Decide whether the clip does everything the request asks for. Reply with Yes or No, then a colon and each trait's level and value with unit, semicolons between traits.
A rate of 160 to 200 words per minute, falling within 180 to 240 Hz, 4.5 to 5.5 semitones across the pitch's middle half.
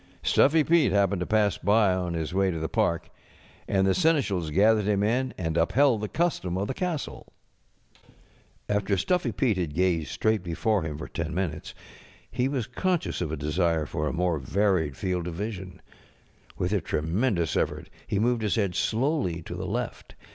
No: average, 180 wpm; very low, 95 Hz; average, 4.9 semitones